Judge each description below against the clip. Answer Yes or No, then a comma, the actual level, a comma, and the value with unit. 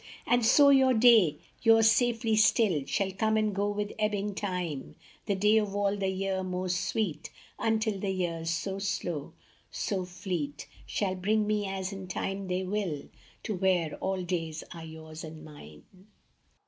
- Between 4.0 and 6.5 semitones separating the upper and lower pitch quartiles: No, average, 3.2 semitones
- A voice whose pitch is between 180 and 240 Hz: Yes, high, 190 Hz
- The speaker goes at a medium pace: Yes, average, 160 wpm